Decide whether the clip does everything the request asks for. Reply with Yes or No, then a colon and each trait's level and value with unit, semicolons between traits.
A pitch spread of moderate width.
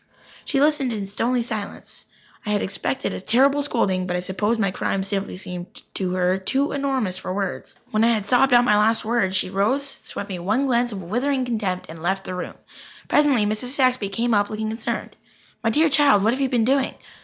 Yes: average, 4.9 semitones